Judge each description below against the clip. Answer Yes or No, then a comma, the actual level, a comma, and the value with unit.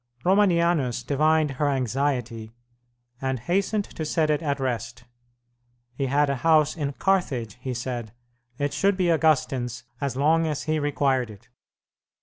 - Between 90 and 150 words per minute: Yes, average, 140 wpm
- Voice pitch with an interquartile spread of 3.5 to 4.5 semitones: Yes, average, 4.1 semitones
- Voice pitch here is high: No, medium, 140 Hz